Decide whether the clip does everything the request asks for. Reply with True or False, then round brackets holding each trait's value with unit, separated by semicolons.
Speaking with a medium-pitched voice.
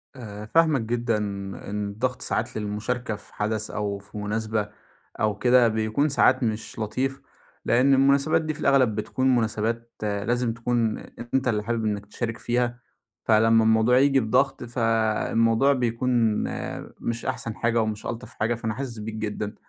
False (115 Hz)